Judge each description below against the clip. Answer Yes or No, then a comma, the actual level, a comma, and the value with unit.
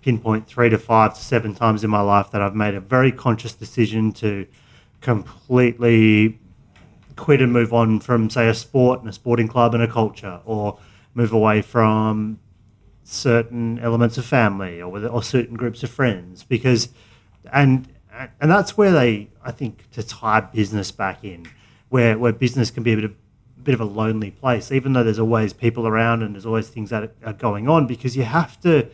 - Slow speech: No, average, 195 wpm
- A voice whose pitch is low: Yes, low, 115 Hz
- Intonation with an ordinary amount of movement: No, narrow, 2.3 semitones